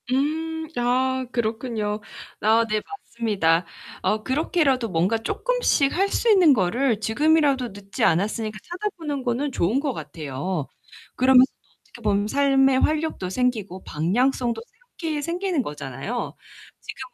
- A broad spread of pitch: Yes, wide, 5.8 semitones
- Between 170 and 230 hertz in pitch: No, very high, 250 Hz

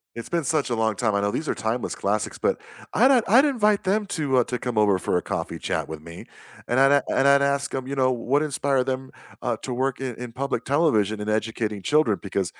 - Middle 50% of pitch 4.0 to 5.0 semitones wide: Yes, average, 4.7 semitones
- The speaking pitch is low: Yes, low, 130 Hz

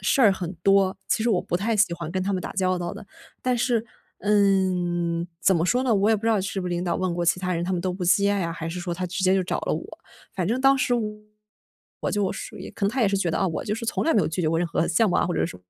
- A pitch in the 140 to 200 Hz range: Yes, medium, 185 Hz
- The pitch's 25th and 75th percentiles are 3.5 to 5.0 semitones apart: No, average, 2.9 semitones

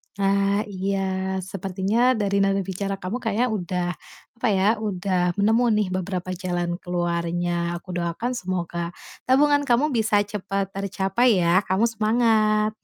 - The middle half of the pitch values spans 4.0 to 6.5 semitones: No, average, 3.0 semitones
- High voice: Yes, high, 195 Hz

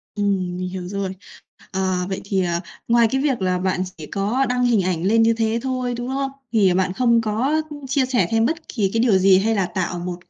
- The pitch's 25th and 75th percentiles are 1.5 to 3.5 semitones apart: No, average, 4.6 semitones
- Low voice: No, high, 205 Hz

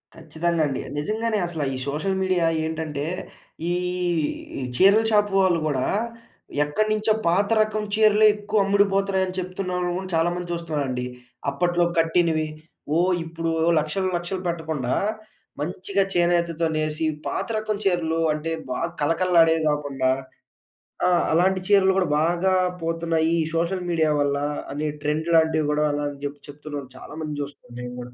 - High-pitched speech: No, medium, 165 Hz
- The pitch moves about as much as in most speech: Yes, average, 3.7 semitones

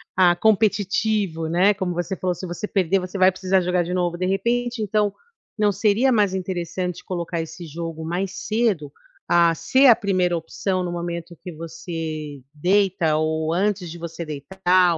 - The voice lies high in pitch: No, medium, 180 Hz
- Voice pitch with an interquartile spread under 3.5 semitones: Yes, average, 2.7 semitones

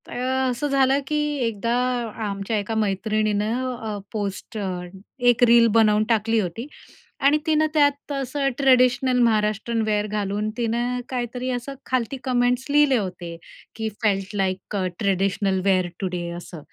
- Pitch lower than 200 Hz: No, high, 225 Hz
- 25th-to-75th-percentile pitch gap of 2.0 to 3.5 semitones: No, average, 3.9 semitones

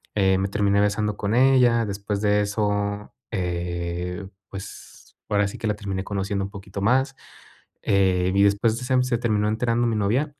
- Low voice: Yes, low, 105 Hz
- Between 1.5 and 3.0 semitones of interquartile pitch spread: Yes, narrow, 2.5 semitones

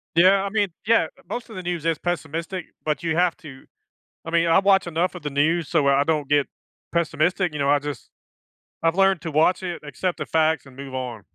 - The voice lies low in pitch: No, medium, 165 Hz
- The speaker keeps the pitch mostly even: No, average, 3.6 semitones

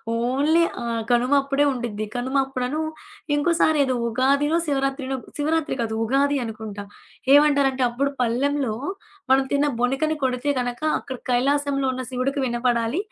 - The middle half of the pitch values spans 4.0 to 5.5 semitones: No, average, 2.8 semitones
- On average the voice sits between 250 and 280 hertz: Yes, very high, 265 Hz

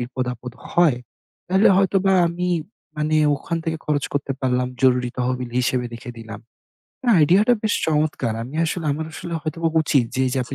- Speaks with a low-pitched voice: No, medium, 145 Hz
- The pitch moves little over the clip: No, average, 5.0 semitones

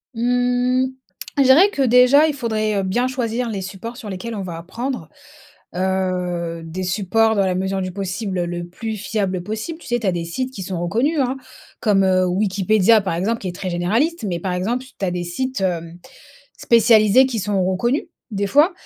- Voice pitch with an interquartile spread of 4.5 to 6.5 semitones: Yes, average, 4.9 semitones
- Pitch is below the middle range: No, high, 205 Hz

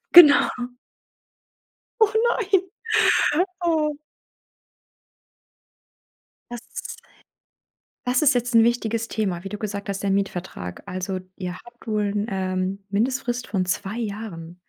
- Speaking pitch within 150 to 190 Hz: No, high, 210 Hz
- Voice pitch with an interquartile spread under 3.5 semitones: No, average, 4.2 semitones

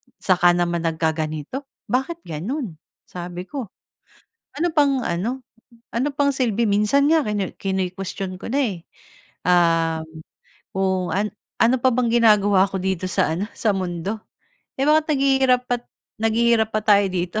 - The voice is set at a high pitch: Yes, high, 205 Hz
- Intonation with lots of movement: Yes, wide, 5.9 semitones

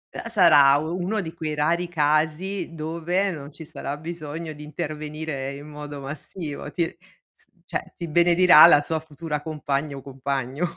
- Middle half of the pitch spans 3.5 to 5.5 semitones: No, narrow, 2.6 semitones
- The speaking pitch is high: No, medium, 155 Hz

